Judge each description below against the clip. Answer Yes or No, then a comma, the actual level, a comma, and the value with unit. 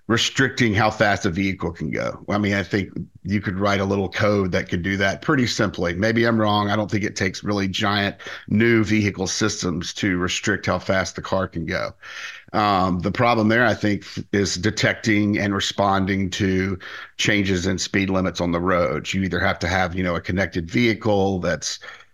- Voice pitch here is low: Yes, low, 100 Hz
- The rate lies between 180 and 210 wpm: Yes, average, 200 wpm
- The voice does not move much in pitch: Yes, narrow, 2.3 semitones